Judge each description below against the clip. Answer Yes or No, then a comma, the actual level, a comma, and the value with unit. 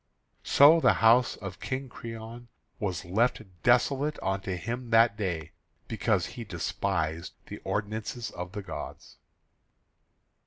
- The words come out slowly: Yes, slow, 120 wpm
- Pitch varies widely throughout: No, average, 4.3 semitones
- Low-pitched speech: Yes, low, 110 Hz